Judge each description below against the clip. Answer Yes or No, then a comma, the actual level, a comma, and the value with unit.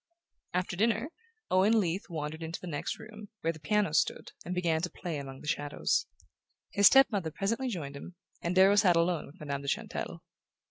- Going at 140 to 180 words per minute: No, average, 190 wpm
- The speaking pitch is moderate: Yes, medium, 175 Hz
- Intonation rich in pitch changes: No, average, 4.4 semitones